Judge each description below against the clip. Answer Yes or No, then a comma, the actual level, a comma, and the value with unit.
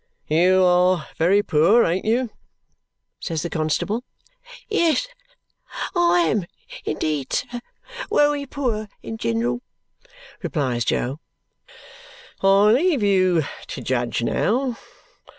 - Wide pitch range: Yes, wide, 7.7 semitones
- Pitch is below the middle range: No, high, 190 Hz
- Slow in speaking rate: Yes, slow, 100 wpm